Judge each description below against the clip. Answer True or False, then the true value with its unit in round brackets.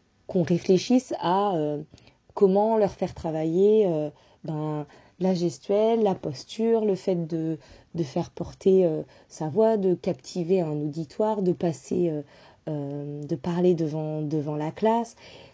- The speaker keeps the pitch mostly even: False (4.3 semitones)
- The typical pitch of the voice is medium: True (175 Hz)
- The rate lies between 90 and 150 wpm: True (145 wpm)